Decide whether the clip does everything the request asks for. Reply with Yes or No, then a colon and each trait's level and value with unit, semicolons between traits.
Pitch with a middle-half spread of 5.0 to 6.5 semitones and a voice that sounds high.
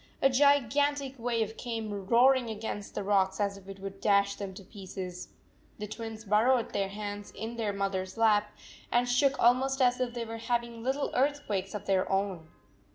No: average, 3.7 semitones; high, 220 Hz